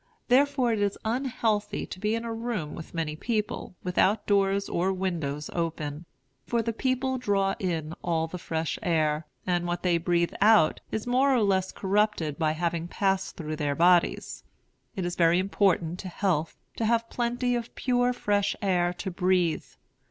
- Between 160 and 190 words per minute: Yes, average, 170 wpm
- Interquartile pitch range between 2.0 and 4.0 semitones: No, average, 4.8 semitones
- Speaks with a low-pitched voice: No, high, 190 Hz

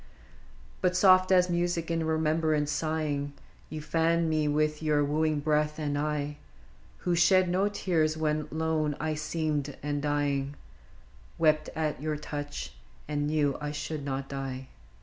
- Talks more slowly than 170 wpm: Yes, average, 145 wpm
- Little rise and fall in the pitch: Yes, narrow, 1.6 semitones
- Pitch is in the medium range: Yes, medium, 155 Hz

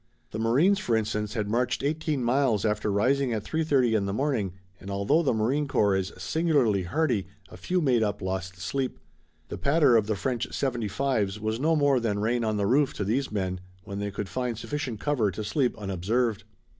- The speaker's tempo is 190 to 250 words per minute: Yes, average, 200 wpm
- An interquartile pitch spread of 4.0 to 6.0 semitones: Yes, average, 5.2 semitones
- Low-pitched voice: Yes, low, 115 Hz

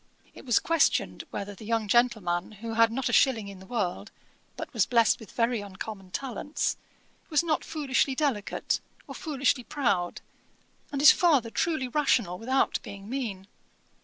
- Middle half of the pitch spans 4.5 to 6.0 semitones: Yes, average, 5.0 semitones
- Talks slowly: No, average, 160 wpm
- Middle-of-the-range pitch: No, high, 230 Hz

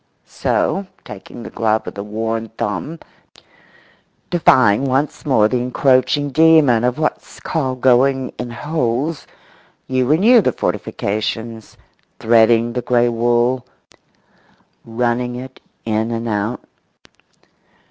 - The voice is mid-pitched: No, low, 120 Hz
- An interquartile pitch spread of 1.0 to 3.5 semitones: Yes, average, 2.9 semitones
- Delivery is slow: Yes, slow, 110 wpm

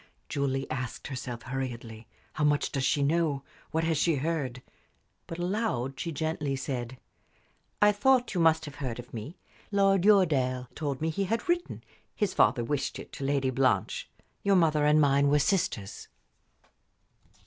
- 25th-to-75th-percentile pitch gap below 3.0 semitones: No, average, 4.3 semitones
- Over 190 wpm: No, average, 160 wpm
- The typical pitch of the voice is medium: Yes, medium, 145 Hz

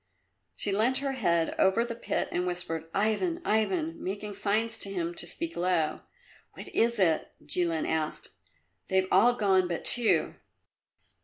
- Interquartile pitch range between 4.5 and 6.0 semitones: Yes, average, 4.8 semitones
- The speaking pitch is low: No, high, 195 Hz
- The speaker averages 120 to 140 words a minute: No, average, 150 wpm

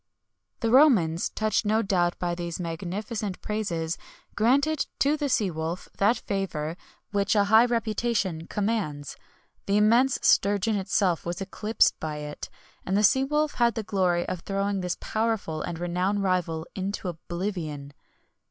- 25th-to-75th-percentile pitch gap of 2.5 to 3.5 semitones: No, average, 4.1 semitones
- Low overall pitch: No, high, 195 Hz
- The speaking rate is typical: Yes, average, 150 wpm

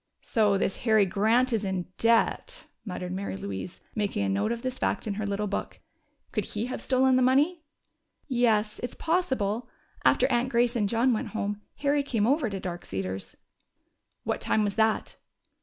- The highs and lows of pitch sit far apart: No, average, 4.0 semitones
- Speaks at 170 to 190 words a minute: Yes, average, 175 wpm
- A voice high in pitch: Yes, high, 220 Hz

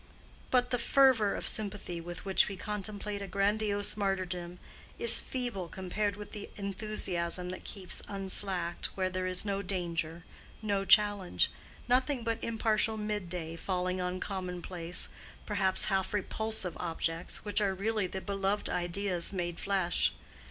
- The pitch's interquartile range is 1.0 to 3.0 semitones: Yes, narrow, 2.6 semitones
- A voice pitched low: No, high, 195 Hz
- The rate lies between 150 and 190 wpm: No, slow, 135 wpm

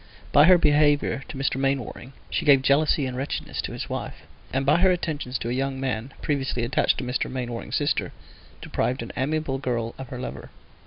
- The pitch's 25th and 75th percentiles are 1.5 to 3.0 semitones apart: Yes, narrow, 2.5 semitones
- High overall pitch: No, low, 135 Hz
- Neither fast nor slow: Yes, average, 195 wpm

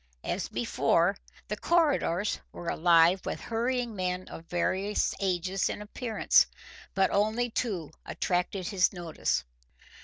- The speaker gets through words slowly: Yes, slow, 120 wpm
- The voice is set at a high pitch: Yes, high, 195 Hz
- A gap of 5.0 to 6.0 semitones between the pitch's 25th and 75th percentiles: No, average, 3.7 semitones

